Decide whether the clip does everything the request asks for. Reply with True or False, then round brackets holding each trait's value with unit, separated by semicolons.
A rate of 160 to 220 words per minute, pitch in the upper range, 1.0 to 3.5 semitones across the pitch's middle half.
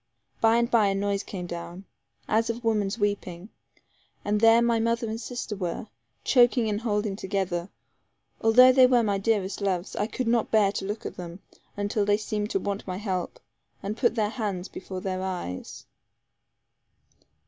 True (170 wpm; 205 Hz; 2.8 semitones)